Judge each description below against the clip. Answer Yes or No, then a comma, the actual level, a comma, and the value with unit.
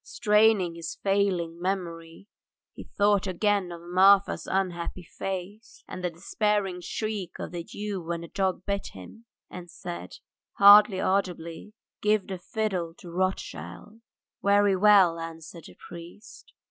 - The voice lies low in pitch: No, medium, 185 Hz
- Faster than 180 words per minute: No, slow, 135 wpm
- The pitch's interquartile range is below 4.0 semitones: Yes, average, 3.1 semitones